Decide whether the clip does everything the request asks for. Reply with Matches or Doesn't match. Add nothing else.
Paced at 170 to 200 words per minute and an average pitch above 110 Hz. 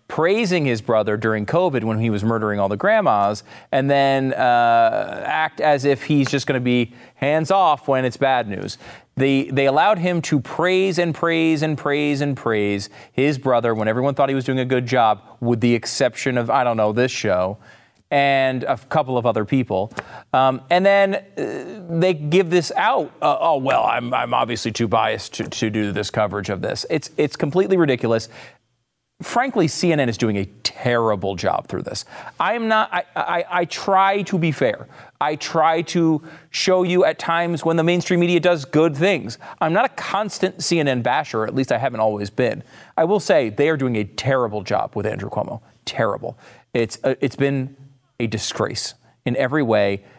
Matches